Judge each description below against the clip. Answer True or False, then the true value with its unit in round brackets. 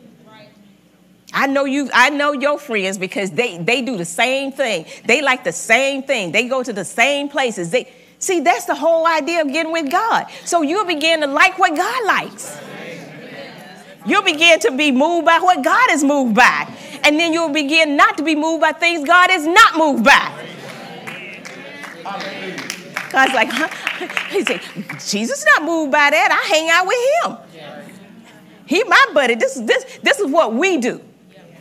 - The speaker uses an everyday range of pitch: False (6.0 semitones)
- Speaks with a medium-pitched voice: False (285 Hz)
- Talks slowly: False (180 wpm)